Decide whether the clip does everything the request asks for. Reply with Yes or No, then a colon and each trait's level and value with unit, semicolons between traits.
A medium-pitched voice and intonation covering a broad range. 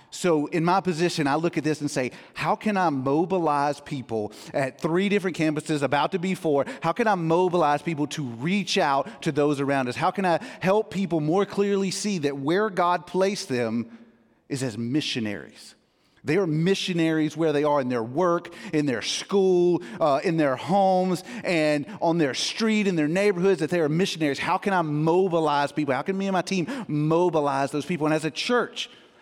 No: medium, 160 Hz; average, 4.4 semitones